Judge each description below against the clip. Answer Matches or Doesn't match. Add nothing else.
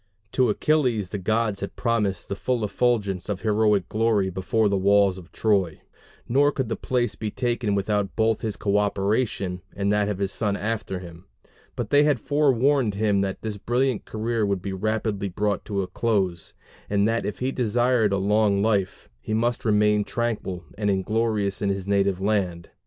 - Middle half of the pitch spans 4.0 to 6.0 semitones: Doesn't match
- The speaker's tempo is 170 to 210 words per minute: Matches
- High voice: Doesn't match